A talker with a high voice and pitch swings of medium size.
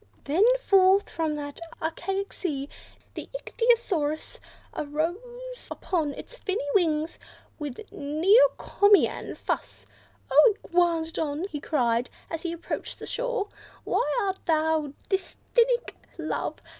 Yes: very high, 340 Hz; average, 5.0 semitones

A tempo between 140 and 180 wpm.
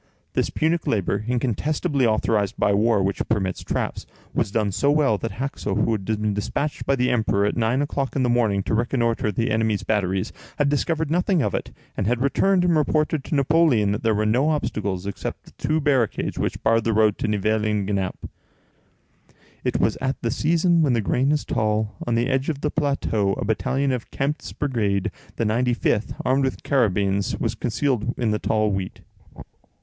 No: average, 195 wpm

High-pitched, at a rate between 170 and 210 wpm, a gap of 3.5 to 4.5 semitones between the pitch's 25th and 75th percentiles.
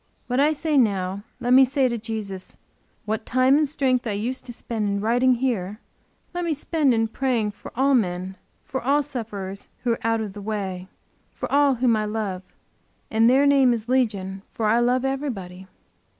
Yes: high, 235 Hz; average, 190 wpm; average, 4.2 semitones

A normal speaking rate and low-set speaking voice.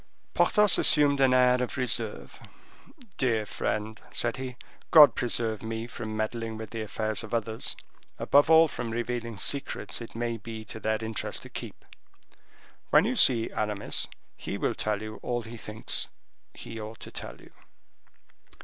Yes: average, 160 wpm; low, 115 Hz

